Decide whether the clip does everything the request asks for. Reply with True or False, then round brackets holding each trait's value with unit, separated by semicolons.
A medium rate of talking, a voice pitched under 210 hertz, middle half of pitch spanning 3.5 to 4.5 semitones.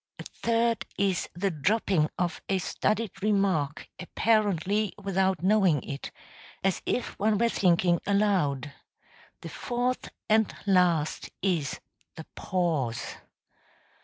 False (110 wpm; 190 Hz; 4.0 semitones)